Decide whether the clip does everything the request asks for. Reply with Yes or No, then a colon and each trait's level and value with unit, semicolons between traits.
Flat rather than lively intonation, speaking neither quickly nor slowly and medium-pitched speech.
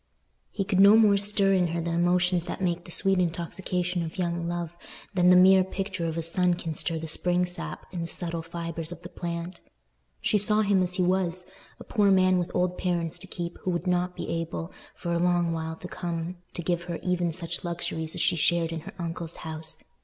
No: narrow, 1.6 semitones; fast, 220 wpm; medium, 175 Hz